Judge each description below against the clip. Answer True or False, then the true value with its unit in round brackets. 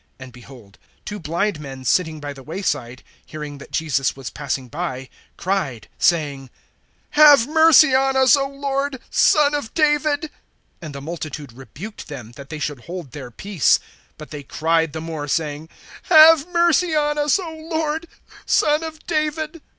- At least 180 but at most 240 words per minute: False (160 wpm)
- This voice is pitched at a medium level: True (170 Hz)